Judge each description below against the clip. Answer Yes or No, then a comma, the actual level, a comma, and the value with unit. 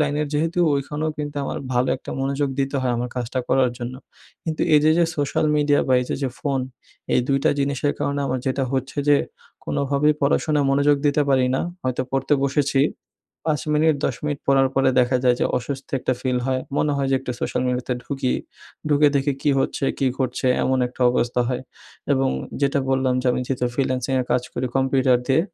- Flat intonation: Yes, narrow, 1.9 semitones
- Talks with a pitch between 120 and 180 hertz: Yes, low, 135 Hz